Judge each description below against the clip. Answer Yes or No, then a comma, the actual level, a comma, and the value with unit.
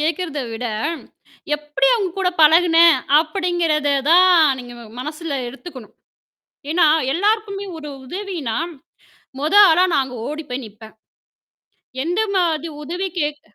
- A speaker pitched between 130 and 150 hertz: No, very high, 320 Hz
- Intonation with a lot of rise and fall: No, average, 3.8 semitones